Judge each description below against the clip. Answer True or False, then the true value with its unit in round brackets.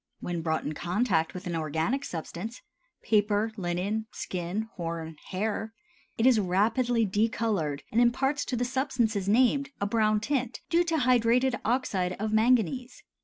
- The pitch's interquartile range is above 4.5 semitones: True (5.4 semitones)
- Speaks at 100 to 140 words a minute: True (135 wpm)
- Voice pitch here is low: False (220 Hz)